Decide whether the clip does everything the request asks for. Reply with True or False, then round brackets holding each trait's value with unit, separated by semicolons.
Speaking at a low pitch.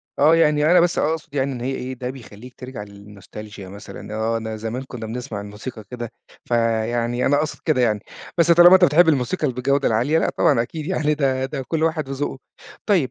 True (130 Hz)